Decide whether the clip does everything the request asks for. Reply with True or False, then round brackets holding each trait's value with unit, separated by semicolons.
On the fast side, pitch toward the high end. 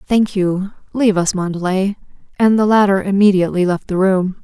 False (160 wpm; 195 Hz)